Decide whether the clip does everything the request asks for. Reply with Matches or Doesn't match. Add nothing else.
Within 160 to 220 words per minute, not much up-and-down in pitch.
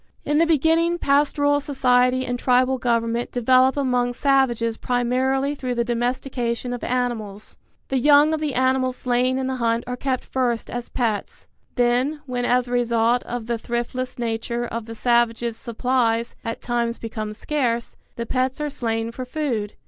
Matches